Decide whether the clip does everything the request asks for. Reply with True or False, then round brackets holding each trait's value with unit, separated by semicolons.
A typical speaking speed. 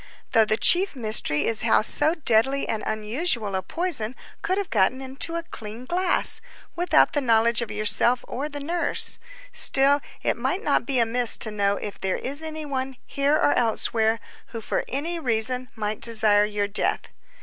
True (175 wpm)